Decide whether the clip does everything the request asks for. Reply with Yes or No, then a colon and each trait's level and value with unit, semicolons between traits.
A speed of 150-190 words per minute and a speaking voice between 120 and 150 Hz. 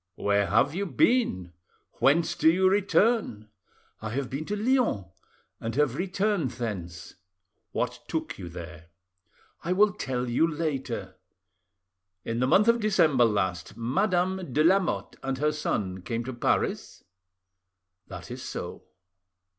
No: slow, 135 wpm; low, 135 Hz